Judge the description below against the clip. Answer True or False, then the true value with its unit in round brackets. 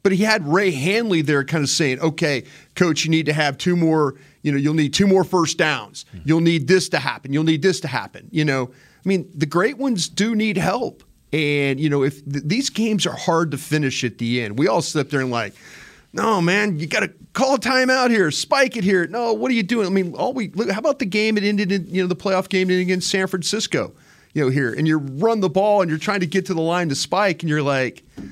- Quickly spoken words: True (260 wpm)